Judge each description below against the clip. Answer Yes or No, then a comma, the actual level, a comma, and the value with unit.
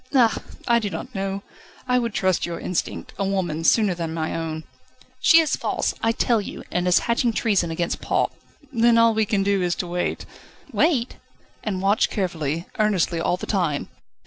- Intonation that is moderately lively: Yes, average, 4.7 semitones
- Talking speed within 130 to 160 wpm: No, average, 185 wpm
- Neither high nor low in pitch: No, high, 195 Hz